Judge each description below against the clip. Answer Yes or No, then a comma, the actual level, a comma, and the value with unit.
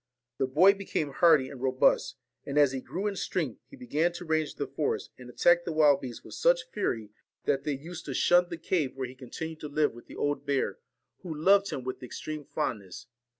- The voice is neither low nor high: Yes, medium, 150 Hz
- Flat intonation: No, average, 4.8 semitones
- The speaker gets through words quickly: Yes, fast, 225 wpm